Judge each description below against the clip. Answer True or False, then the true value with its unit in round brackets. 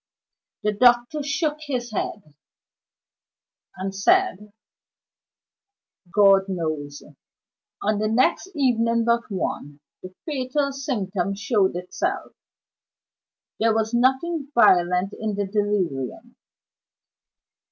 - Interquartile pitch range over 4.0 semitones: True (4.8 semitones)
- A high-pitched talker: True (215 Hz)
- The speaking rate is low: True (90 wpm)